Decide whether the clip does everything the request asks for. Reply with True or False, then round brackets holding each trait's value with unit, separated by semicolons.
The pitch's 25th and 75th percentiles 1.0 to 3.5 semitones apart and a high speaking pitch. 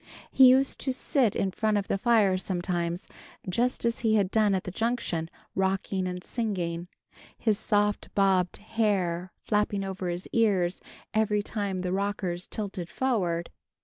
True (3.2 semitones; 195 Hz)